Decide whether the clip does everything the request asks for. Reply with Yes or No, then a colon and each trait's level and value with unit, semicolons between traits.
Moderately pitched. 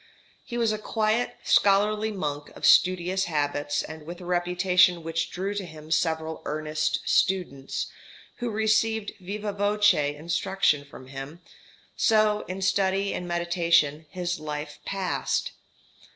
Yes: medium, 180 Hz